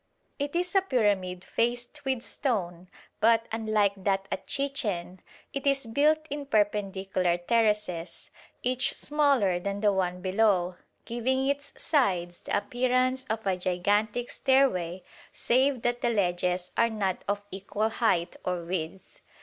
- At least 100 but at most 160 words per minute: Yes, slow, 135 wpm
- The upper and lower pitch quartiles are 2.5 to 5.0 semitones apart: No, wide, 5.6 semitones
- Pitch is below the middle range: No, high, 215 Hz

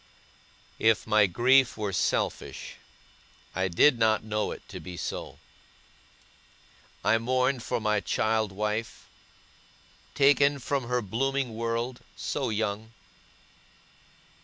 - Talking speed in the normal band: No, slow, 110 wpm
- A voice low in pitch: Yes, low, 115 Hz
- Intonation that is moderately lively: Yes, average, 3.1 semitones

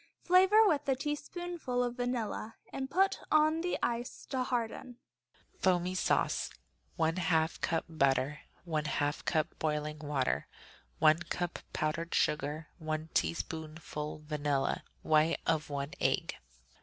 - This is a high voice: No, medium, 165 Hz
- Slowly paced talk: Yes, slow, 120 wpm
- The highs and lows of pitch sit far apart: Yes, wide, 8.6 semitones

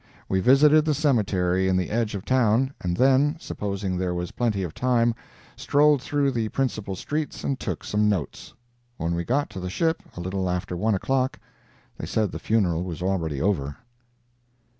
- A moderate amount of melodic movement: No, wide, 6.3 semitones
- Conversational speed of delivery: Yes, average, 180 wpm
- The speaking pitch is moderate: No, low, 105 Hz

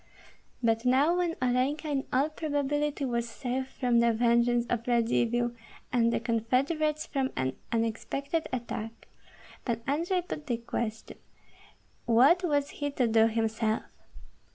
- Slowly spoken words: Yes, slow, 130 wpm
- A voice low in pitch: No, high, 245 Hz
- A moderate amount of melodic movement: Yes, average, 3.8 semitones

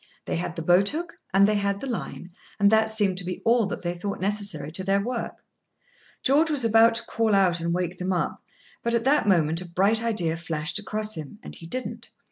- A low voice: No, high, 200 Hz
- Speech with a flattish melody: No, average, 4.3 semitones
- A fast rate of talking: Yes, fast, 225 wpm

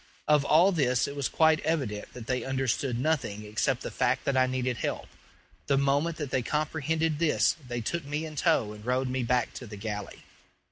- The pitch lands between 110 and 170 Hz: Yes, low, 135 Hz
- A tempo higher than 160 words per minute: Yes, average, 195 wpm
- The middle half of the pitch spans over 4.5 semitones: No, average, 3.9 semitones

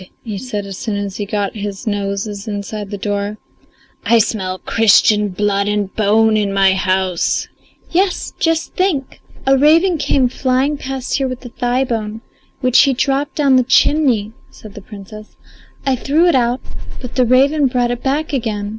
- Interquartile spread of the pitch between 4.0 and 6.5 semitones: Yes, average, 4.7 semitones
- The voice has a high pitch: Yes, high, 225 Hz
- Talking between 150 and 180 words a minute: Yes, average, 170 wpm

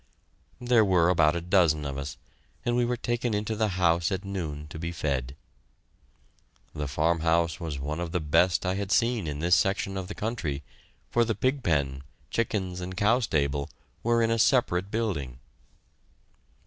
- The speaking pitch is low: Yes, very low, 90 Hz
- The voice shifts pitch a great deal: Yes, wide, 6.1 semitones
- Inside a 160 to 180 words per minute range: Yes, average, 175 wpm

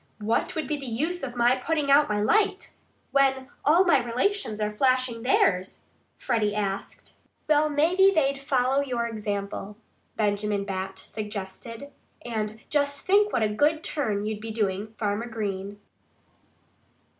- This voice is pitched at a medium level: No, high, 235 Hz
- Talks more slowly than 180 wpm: Yes, average, 145 wpm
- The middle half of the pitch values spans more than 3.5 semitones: Yes, wide, 5.4 semitones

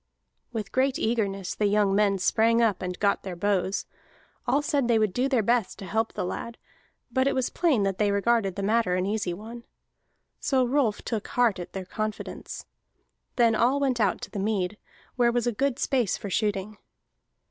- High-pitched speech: Yes, high, 220 Hz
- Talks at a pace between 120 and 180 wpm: No, average, 190 wpm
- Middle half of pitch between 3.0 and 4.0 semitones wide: Yes, average, 3.5 semitones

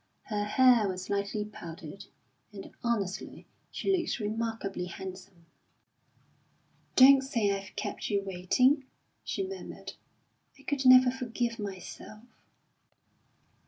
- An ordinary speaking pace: No, slow, 105 wpm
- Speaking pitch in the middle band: No, high, 210 Hz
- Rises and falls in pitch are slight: No, average, 4.6 semitones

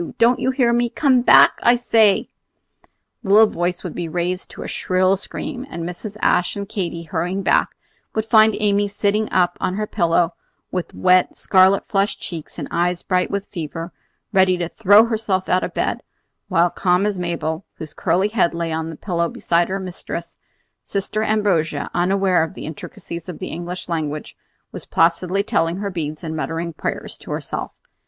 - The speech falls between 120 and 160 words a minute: No, average, 180 wpm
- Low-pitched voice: No, medium, 185 Hz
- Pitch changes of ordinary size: Yes, average, 3.2 semitones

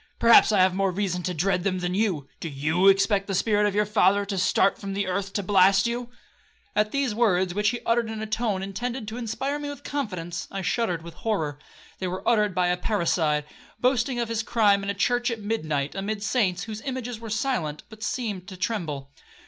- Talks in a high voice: Yes, high, 200 Hz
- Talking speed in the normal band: No, fast, 215 wpm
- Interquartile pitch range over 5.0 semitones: No, average, 3.7 semitones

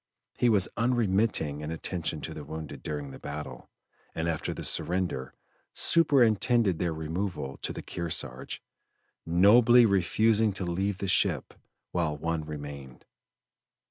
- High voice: No, very low, 85 Hz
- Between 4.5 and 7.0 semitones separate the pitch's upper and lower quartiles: Yes, average, 5.2 semitones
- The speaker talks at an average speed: No, slow, 130 wpm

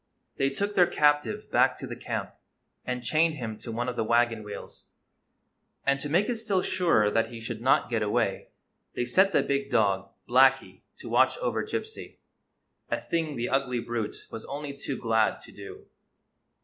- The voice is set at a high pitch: No, low, 130 Hz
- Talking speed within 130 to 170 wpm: No, average, 185 wpm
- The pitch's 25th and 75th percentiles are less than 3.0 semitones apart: No, average, 5.2 semitones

